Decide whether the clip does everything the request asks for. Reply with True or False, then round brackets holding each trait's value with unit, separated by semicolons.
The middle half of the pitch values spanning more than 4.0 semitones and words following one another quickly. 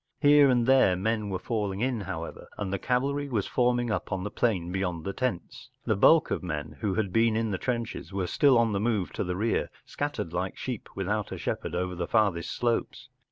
True (4.6 semitones; 215 wpm)